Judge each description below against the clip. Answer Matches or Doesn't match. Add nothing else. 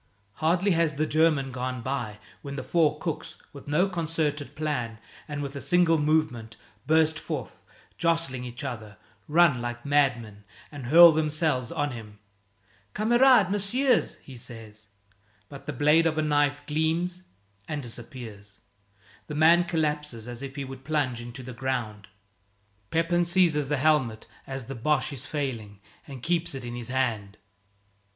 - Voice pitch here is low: Doesn't match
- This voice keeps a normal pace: Matches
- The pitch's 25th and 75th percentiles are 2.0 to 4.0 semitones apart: Doesn't match